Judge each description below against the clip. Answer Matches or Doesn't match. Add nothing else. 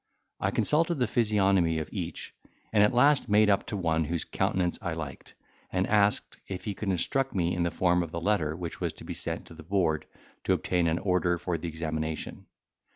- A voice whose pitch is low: Matches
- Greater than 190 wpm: Matches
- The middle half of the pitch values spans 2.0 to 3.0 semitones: Doesn't match